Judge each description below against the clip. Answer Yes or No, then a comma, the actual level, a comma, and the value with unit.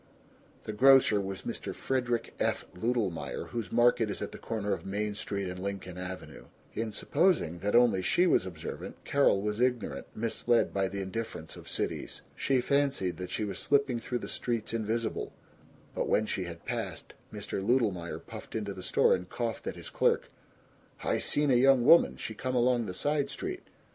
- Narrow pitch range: No, average, 4.3 semitones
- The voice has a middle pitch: No, low, 110 Hz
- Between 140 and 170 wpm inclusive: No, average, 180 wpm